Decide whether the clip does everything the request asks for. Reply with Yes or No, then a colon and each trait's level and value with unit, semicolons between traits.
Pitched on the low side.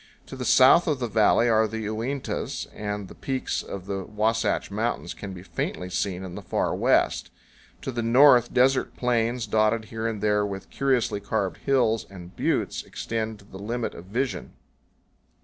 Yes: low, 110 Hz